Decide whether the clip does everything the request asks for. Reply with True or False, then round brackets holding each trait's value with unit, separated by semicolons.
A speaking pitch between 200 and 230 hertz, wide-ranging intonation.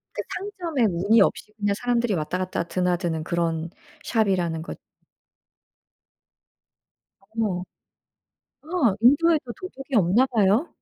True (210 Hz; 6.5 semitones)